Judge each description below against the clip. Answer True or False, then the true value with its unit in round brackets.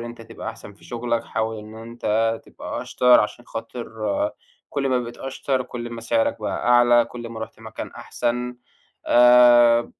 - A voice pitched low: True (120 Hz)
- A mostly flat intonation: True (1.2 semitones)